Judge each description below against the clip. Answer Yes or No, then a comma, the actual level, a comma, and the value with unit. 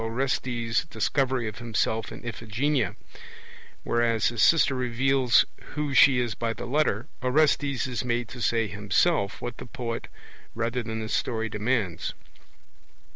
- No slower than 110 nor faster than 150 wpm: Yes, slow, 135 wpm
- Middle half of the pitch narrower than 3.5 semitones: Yes, narrow, 2.6 semitones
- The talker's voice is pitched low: Yes, low, 120 Hz